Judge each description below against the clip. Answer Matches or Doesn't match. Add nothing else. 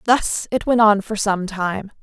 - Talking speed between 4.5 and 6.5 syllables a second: Doesn't match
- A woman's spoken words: Matches